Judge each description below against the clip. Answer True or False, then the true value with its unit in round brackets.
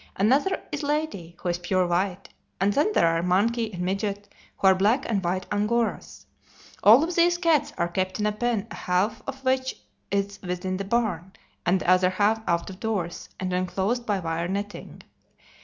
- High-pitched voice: True (200 Hz)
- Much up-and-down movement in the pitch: False (4.3 semitones)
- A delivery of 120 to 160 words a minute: False (185 wpm)